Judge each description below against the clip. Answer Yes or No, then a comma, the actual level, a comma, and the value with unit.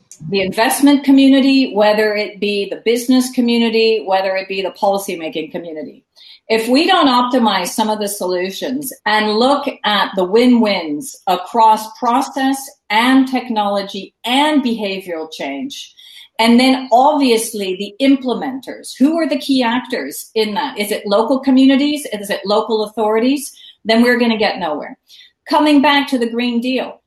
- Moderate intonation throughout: Yes, average, 4.5 semitones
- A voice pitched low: No, high, 235 Hz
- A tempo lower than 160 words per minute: Yes, average, 150 wpm